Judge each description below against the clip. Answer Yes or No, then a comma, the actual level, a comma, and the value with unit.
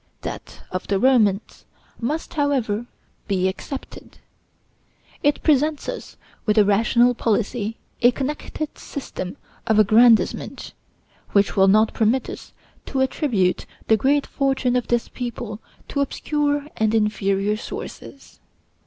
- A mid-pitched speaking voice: No, high, 235 Hz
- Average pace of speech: No, slow, 120 wpm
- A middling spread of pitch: Yes, average, 4.4 semitones